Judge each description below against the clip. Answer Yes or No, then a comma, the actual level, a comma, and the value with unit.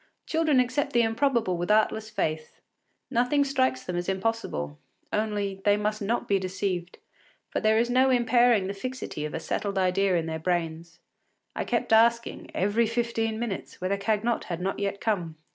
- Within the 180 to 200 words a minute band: No, average, 170 wpm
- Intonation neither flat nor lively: Yes, average, 4.2 semitones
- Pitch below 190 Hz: No, high, 210 Hz